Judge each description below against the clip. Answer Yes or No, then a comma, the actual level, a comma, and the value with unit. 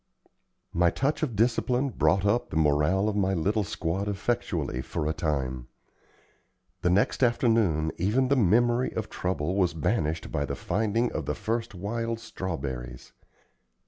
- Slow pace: No, average, 145 wpm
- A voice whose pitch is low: Yes, low, 100 Hz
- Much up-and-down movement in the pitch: Yes, wide, 6.5 semitones